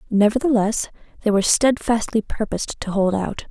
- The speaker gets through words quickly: No, slow, 135 wpm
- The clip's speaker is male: No, female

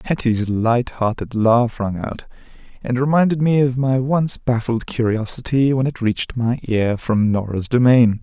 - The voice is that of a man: Yes, male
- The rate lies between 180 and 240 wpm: No, average, 155 wpm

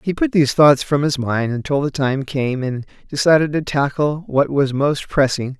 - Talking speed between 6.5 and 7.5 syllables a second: No, 4.8 syllables/s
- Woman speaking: No, male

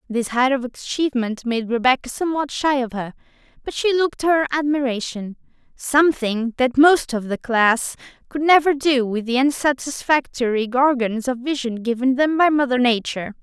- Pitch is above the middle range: Yes, very high, 260 Hz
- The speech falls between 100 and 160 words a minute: Yes, average, 155 wpm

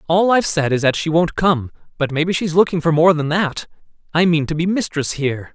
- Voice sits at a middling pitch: Yes, medium, 160 Hz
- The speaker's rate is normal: No, fast, 225 wpm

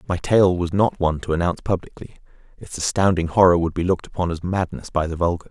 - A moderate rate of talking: No, fast, 220 wpm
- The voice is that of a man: Yes, male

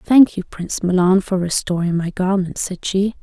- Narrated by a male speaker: No, female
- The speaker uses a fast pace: No, average, 185 wpm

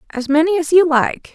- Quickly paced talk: Yes, fast, 225 wpm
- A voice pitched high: Yes, very high, 315 Hz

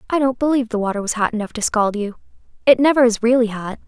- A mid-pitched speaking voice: No, high, 235 Hz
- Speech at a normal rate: No, fast, 250 wpm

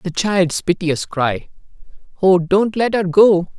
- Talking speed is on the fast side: No, average, 150 wpm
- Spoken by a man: Yes, male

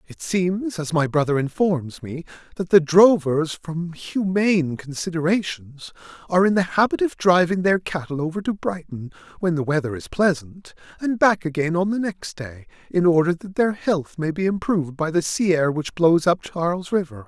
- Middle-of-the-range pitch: Yes, medium, 170 Hz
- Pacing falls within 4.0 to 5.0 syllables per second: Yes, 4.6 syllables/s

